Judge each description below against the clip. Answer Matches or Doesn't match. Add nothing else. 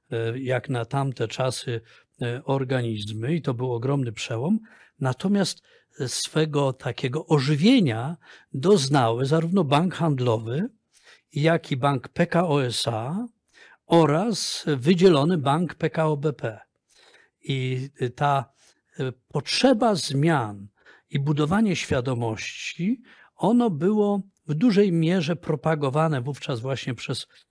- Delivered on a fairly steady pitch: Doesn't match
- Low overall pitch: Doesn't match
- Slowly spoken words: Matches